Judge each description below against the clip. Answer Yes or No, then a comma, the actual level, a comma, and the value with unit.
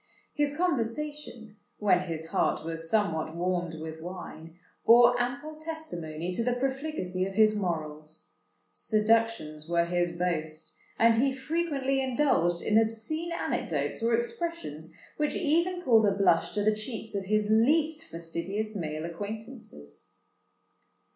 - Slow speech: Yes, slow, 130 wpm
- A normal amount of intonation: No, wide, 7.8 semitones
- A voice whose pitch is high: Yes, high, 215 Hz